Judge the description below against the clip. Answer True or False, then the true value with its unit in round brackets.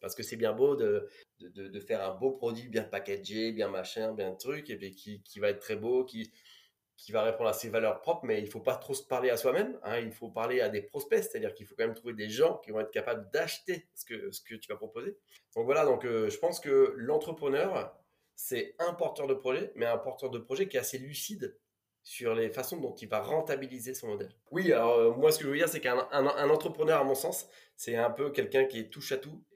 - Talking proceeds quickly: True (260 wpm)